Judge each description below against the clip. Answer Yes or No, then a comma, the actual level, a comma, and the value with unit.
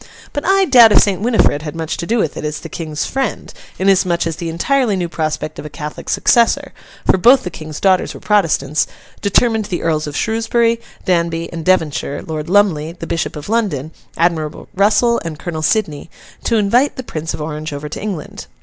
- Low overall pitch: No, medium, 170 Hz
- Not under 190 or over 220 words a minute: Yes, average, 195 wpm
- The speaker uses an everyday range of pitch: No, wide, 5.7 semitones